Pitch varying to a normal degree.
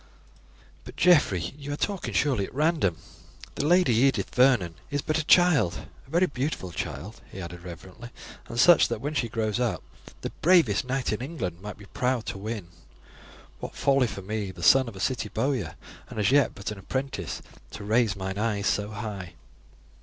No: wide, 5.8 semitones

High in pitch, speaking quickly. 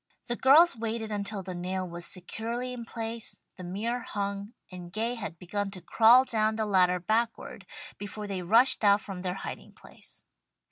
No: high, 210 Hz; average, 175 wpm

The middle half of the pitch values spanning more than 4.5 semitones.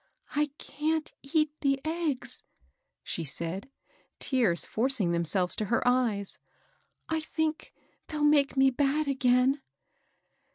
Yes: average, 5.3 semitones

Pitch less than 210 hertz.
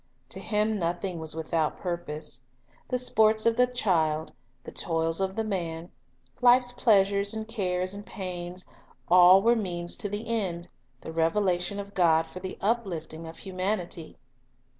Yes: medium, 185 Hz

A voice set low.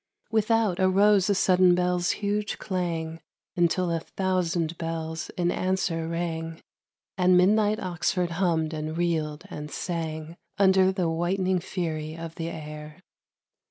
No: medium, 175 Hz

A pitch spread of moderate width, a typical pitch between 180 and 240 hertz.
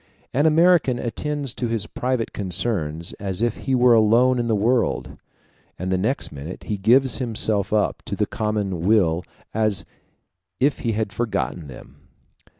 No: average, 4.6 semitones; low, 110 Hz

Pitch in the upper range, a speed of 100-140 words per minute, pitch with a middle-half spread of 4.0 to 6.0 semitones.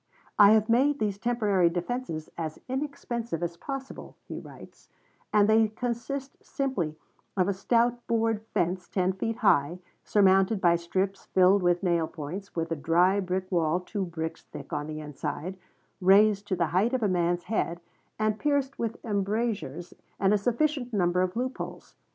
No: high, 195 Hz; average, 165 wpm; average, 4.7 semitones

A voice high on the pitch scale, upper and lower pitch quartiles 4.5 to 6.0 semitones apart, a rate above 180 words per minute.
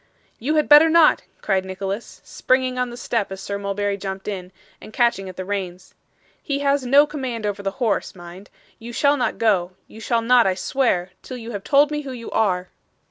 Yes: high, 225 Hz; average, 5.1 semitones; fast, 205 wpm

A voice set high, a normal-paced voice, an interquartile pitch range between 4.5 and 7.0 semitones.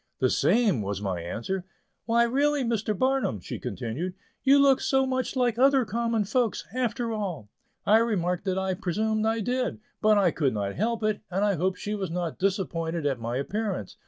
Yes: high, 205 Hz; average, 185 wpm; wide, 5.6 semitones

